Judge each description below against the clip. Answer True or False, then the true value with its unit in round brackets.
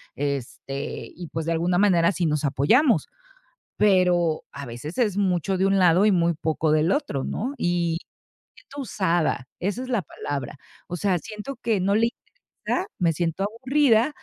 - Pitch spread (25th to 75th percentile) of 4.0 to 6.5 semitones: True (4.8 semitones)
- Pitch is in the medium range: True (180 Hz)